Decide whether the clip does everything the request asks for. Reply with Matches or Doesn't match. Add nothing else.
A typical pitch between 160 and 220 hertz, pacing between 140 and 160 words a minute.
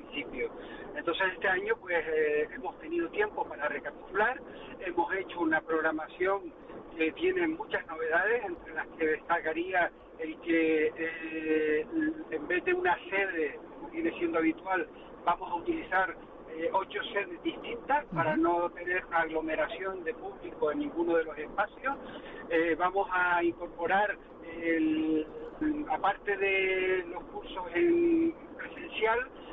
Doesn't match